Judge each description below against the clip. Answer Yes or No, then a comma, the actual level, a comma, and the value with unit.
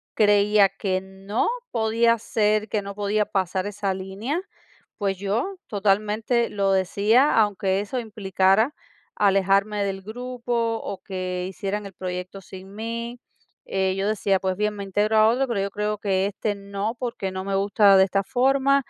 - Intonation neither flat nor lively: No, narrow, 2.3 semitones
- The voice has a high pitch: Yes, high, 205 Hz